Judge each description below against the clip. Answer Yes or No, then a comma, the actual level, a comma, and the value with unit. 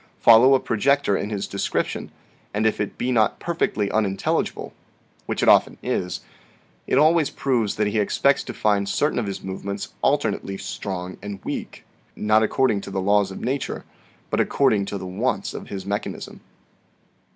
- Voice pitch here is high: No, low, 105 Hz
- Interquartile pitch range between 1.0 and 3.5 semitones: No, average, 4.0 semitones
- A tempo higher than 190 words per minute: No, average, 165 wpm